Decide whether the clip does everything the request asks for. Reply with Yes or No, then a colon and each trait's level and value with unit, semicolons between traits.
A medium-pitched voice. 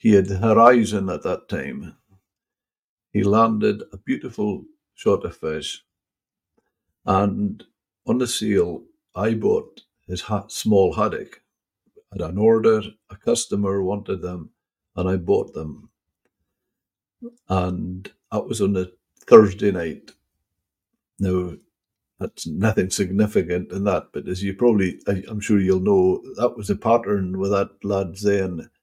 No: low, 100 Hz